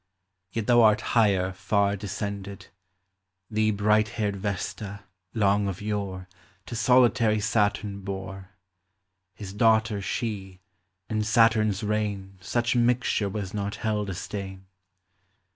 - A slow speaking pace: Yes, slow, 120 wpm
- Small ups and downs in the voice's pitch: Yes, narrow, 1.9 semitones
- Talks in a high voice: No, low, 105 Hz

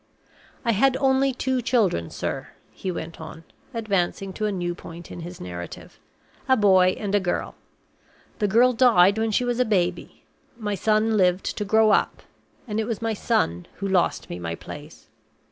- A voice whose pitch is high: Yes, high, 205 Hz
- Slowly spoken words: No, average, 180 wpm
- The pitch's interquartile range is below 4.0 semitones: No, average, 4.3 semitones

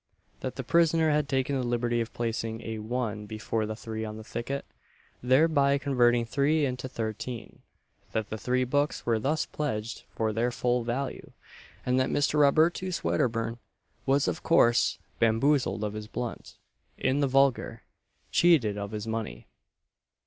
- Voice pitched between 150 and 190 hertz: No, low, 120 Hz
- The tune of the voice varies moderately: Yes, average, 3.8 semitones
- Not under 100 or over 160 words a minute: Yes, average, 155 wpm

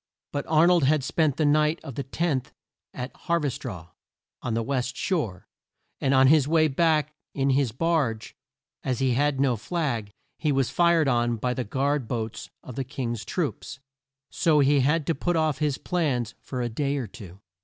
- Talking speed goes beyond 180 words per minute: Yes, average, 190 wpm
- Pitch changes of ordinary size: Yes, average, 3.9 semitones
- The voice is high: No, low, 135 Hz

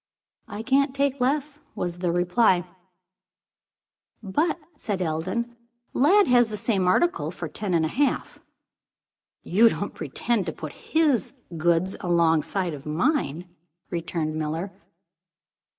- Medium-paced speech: No, slow, 120 wpm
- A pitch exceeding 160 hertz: Yes, high, 190 Hz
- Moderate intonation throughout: No, wide, 7.2 semitones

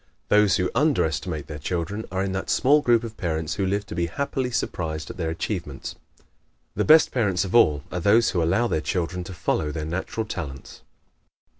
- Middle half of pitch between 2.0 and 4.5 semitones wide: No, average, 5.3 semitones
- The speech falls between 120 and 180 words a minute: No, average, 195 wpm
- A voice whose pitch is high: No, very low, 95 Hz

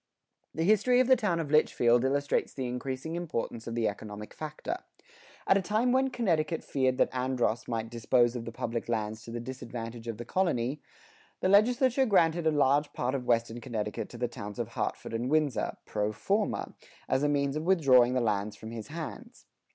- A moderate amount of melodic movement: No, wide, 6.1 semitones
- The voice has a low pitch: Yes, low, 130 Hz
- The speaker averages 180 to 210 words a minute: Yes, average, 190 wpm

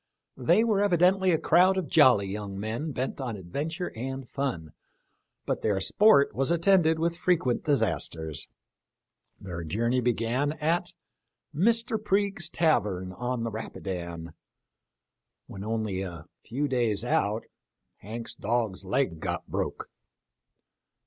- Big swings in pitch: Yes, wide, 8.6 semitones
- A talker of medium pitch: No, low, 125 Hz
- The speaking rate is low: Yes, slow, 130 wpm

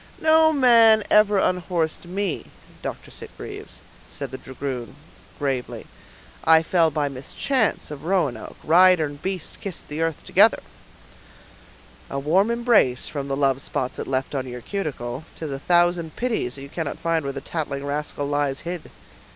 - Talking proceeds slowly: No, average, 155 wpm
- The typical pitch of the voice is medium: Yes, medium, 160 Hz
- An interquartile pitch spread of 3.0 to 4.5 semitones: No, average, 5.2 semitones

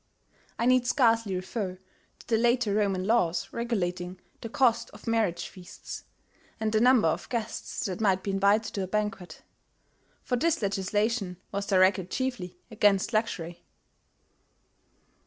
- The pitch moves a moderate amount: Yes, average, 3.7 semitones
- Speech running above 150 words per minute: No, average, 140 wpm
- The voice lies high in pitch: Yes, high, 210 Hz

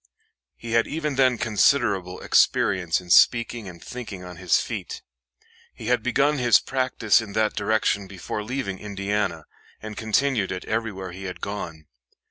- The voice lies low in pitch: Yes, low, 105 Hz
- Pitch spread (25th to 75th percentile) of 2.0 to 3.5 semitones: No, average, 4.2 semitones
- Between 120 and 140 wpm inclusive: No, average, 150 wpm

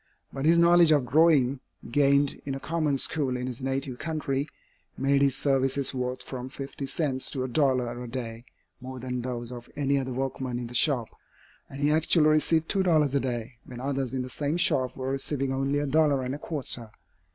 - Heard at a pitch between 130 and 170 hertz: Yes, low, 135 Hz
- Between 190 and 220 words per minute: Yes, average, 200 wpm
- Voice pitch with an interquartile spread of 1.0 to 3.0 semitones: Yes, narrow, 2.4 semitones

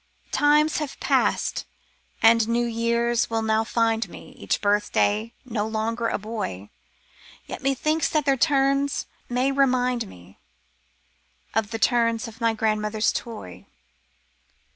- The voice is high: Yes, high, 230 Hz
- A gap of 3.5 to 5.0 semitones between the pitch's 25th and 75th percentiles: No, average, 2.7 semitones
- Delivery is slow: Yes, slow, 125 wpm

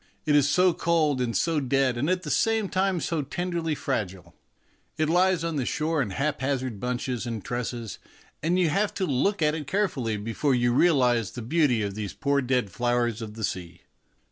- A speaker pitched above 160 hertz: No, low, 135 Hz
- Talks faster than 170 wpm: Yes, average, 195 wpm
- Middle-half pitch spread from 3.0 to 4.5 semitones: No, wide, 5.6 semitones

